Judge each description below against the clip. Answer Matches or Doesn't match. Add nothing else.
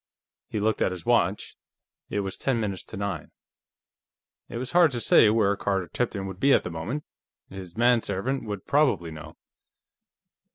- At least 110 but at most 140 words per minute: Doesn't match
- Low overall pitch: Matches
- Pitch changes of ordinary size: Matches